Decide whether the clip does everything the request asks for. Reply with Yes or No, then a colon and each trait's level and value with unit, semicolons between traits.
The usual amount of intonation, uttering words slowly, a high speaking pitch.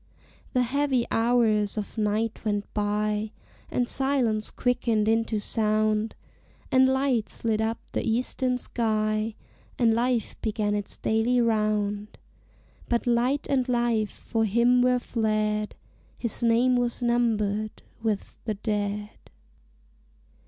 No: narrow, 2.3 semitones; slow, 115 wpm; high, 225 Hz